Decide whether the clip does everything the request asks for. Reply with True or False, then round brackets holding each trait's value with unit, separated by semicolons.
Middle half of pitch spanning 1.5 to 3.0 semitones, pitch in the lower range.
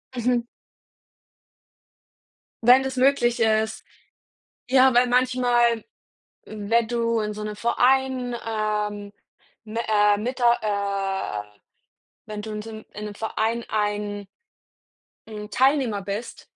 False (2.6 semitones; 220 Hz)